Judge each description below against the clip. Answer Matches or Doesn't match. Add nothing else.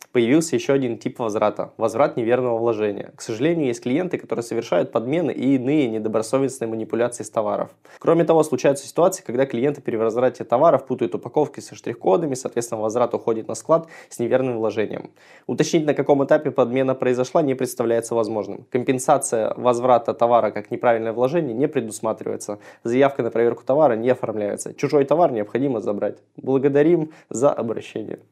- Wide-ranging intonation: Doesn't match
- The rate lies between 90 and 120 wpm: Doesn't match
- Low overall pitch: Matches